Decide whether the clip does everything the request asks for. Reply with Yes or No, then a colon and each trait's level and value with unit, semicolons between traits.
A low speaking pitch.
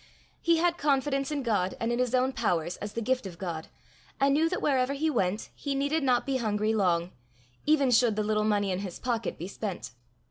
No: high, 235 Hz